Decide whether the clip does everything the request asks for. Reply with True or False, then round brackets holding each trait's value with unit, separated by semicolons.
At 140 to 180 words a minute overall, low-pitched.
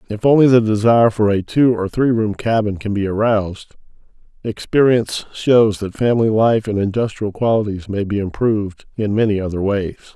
True (170 wpm; 105 Hz)